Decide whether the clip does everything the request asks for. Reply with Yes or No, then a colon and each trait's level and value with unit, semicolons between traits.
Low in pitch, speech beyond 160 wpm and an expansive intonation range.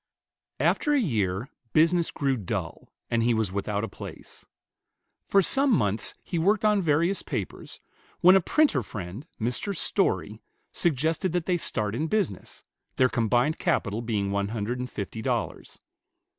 No: low, 125 Hz; average, 150 wpm; wide, 8.5 semitones